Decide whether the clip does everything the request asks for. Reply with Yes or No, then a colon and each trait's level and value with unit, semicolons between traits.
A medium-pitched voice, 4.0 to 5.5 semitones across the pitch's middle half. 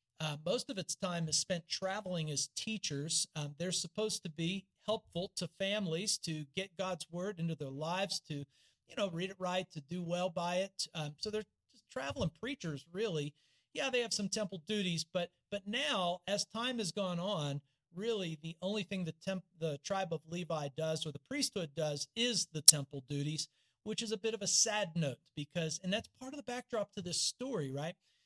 Yes: medium, 180 Hz; average, 4.4 semitones